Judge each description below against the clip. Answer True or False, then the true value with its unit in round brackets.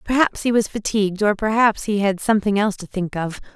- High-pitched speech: True (205 Hz)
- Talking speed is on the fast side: True (220 wpm)